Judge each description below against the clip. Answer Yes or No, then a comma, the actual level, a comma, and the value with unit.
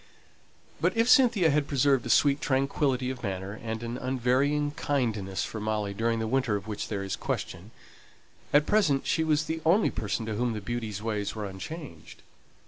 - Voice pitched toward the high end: No, low, 120 Hz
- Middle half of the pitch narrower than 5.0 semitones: No, wide, 5.4 semitones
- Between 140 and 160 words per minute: No, average, 180 wpm